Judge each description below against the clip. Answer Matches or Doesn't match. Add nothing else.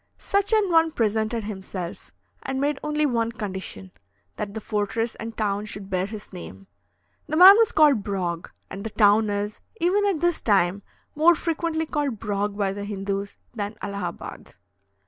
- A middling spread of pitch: Doesn't match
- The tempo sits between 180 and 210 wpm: Doesn't match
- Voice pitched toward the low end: Doesn't match